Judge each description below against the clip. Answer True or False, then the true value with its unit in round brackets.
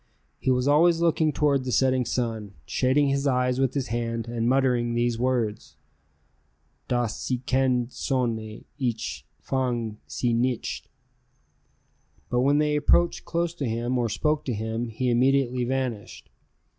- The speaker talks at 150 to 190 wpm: False (140 wpm)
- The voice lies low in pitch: True (125 Hz)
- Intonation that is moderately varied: False (2.3 semitones)